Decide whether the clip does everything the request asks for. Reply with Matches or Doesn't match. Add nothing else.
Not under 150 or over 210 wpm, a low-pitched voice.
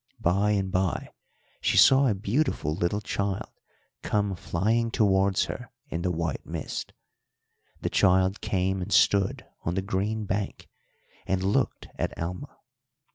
Doesn't match